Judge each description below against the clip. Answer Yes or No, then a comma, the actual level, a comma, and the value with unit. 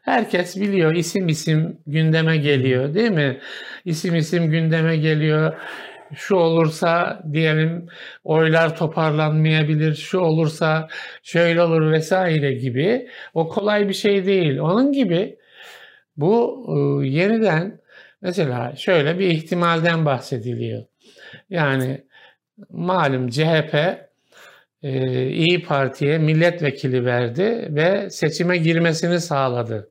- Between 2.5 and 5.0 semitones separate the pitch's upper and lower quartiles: Yes, average, 3.3 semitones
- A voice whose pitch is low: No, medium, 160 Hz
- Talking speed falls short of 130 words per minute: Yes, slow, 95 wpm